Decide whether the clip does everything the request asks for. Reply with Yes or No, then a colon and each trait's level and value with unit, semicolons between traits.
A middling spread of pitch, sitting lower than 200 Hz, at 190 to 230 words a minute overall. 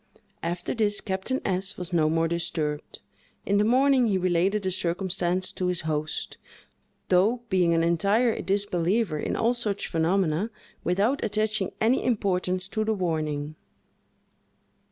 No: average, 3.8 semitones; medium, 185 Hz; slow, 135 wpm